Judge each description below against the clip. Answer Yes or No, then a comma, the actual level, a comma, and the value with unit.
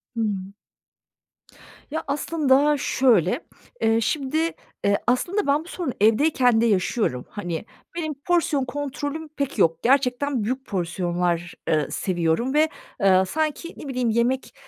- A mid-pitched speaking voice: No, very high, 255 Hz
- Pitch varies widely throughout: Yes, wide, 6.4 semitones